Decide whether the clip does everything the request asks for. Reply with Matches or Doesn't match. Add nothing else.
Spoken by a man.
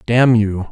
Matches